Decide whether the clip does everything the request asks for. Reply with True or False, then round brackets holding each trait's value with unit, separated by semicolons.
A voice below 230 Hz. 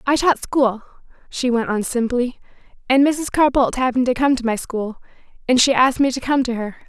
False (250 Hz)